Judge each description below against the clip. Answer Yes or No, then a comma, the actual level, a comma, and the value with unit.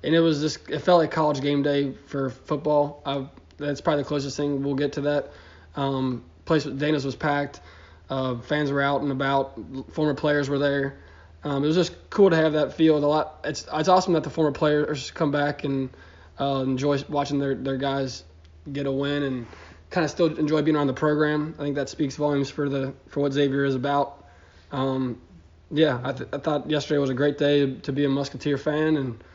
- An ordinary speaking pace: No, fast, 215 wpm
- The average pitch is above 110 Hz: Yes, medium, 140 Hz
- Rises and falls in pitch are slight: Yes, narrow, 2.1 semitones